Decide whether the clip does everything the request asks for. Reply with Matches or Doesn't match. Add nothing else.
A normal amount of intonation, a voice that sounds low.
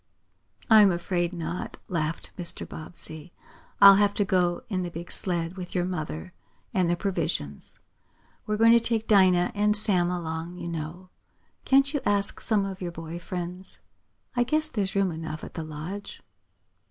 Doesn't match